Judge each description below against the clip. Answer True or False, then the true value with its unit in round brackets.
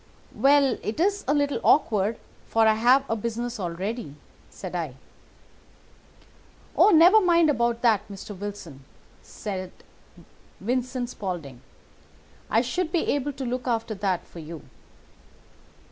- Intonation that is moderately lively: False (5.8 semitones)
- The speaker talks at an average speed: False (130 wpm)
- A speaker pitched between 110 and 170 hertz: False (230 Hz)